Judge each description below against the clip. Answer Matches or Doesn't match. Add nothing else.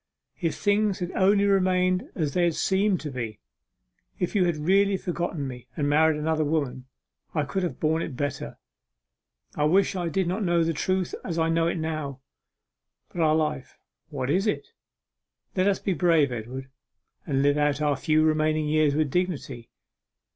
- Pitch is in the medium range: Matches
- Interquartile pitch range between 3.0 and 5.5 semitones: Matches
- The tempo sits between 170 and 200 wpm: Matches